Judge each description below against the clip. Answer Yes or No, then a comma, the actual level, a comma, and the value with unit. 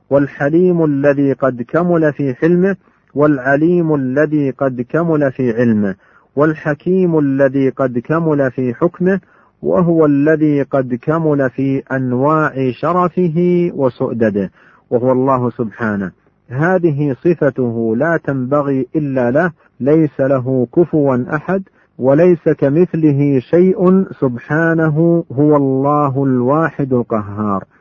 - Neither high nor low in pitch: Yes, medium, 145 Hz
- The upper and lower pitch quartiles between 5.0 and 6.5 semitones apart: No, average, 3.8 semitones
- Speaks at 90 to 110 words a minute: Yes, average, 100 wpm